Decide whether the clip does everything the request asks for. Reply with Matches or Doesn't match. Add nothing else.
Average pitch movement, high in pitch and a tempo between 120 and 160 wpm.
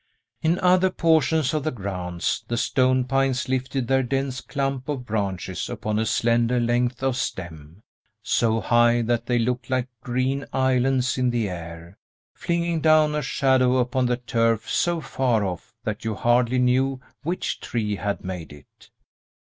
Doesn't match